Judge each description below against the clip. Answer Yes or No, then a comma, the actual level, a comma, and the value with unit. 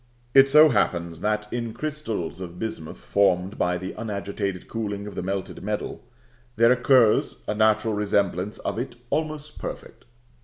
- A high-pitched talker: No, low, 105 Hz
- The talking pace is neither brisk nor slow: Yes, average, 150 wpm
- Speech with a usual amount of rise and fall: Yes, average, 3.7 semitones